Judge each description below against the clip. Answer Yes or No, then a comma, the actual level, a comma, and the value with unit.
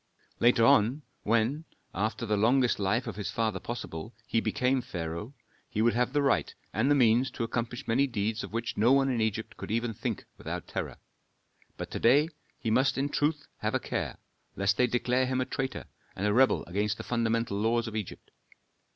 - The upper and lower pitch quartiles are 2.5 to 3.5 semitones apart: Yes, average, 2.9 semitones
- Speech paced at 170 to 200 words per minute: Yes, average, 195 wpm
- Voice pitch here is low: Yes, low, 115 Hz